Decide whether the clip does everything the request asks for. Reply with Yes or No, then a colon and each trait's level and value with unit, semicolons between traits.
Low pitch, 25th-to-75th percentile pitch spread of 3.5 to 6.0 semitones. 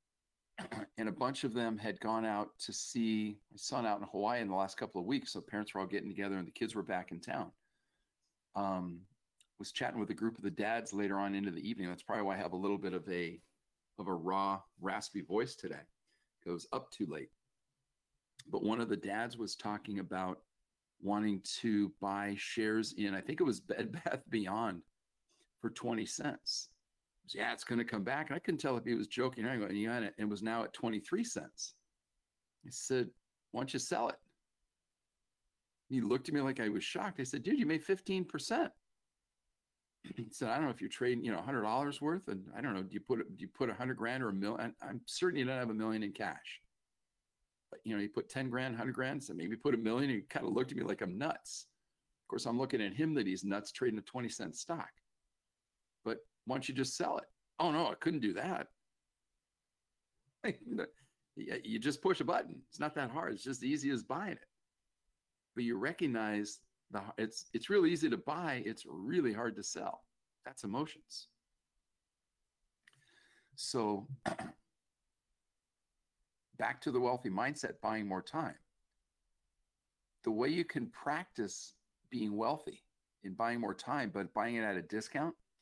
Yes: low, 105 Hz; average, 4.3 semitones